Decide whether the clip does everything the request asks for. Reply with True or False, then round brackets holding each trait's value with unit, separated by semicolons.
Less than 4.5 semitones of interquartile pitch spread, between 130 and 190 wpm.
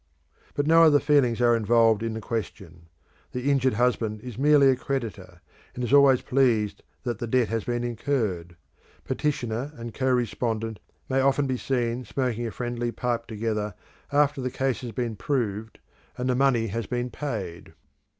True (2.9 semitones; 170 wpm)